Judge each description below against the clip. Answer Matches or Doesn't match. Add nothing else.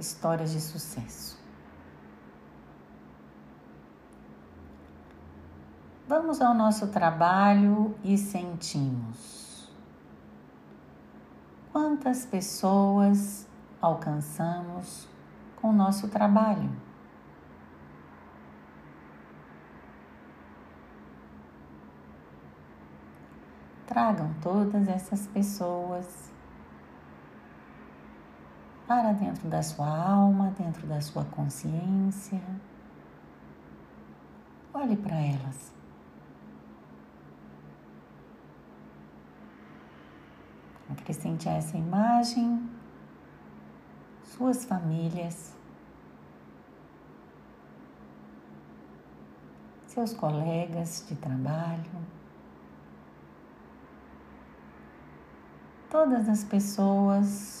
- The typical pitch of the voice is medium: Matches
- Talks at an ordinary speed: Doesn't match